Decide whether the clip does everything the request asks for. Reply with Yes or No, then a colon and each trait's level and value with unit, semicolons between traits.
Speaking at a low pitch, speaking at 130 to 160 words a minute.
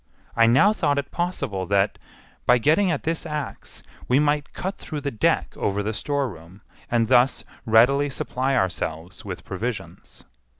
Yes: low, 125 Hz; average, 155 wpm